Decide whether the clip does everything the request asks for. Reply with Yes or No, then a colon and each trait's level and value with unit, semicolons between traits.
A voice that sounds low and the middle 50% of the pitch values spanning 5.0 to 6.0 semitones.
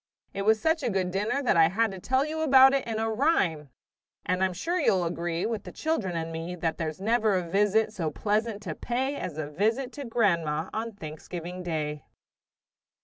No: high, 200 Hz; wide, 5.6 semitones